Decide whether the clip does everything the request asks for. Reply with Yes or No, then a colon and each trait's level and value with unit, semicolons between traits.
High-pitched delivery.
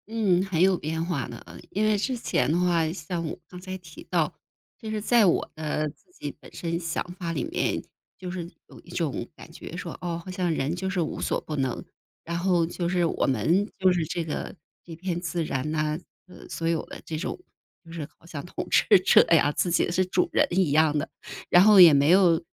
No: medium, 170 Hz